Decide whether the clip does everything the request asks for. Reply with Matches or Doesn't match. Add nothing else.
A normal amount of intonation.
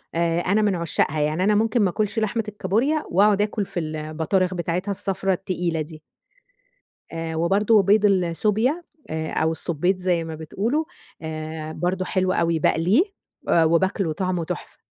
Matches